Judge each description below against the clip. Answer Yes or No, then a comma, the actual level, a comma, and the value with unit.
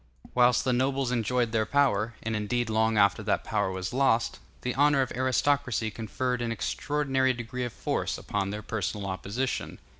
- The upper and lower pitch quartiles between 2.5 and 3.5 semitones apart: Yes, average, 3.1 semitones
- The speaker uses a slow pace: No, average, 170 wpm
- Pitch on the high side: No, low, 120 Hz